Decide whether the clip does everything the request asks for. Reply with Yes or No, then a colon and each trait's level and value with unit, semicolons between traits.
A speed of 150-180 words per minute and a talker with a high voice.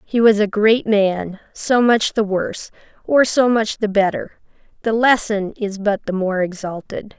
Yes: average, 175 wpm; high, 210 Hz